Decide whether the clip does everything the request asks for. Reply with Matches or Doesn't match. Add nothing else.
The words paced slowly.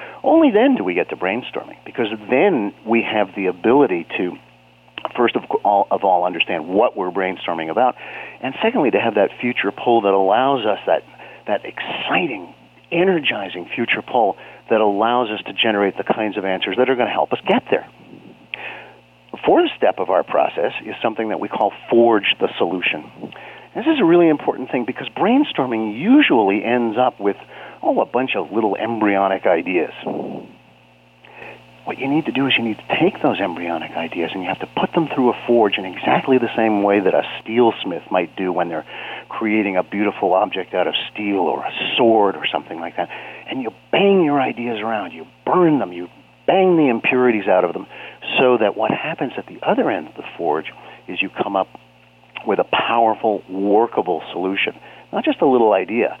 Doesn't match